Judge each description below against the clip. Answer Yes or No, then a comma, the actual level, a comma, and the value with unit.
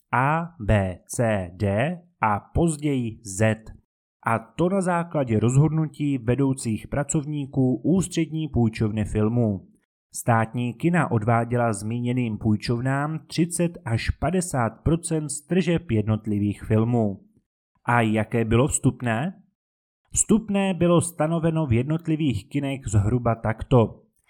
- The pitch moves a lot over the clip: Yes, wide, 6.2 semitones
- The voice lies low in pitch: Yes, low, 125 Hz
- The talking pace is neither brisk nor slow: No, slow, 100 wpm